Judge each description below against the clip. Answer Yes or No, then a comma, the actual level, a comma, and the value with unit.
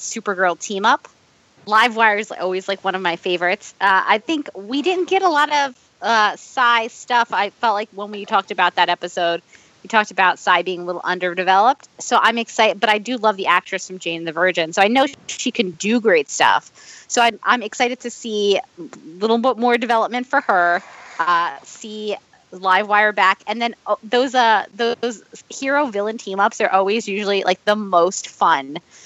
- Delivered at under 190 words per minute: No, average, 195 wpm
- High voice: Yes, high, 210 Hz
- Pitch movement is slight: No, average, 4.3 semitones